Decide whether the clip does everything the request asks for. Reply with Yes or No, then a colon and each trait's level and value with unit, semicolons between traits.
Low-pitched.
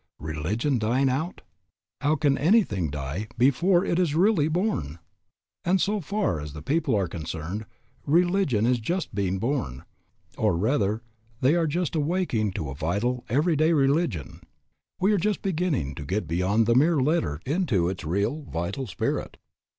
Yes: low, 130 Hz